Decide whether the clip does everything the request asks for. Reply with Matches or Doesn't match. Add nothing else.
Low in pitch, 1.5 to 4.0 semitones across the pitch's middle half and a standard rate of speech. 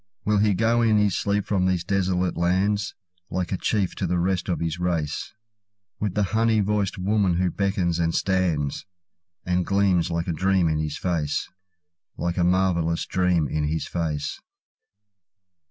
Matches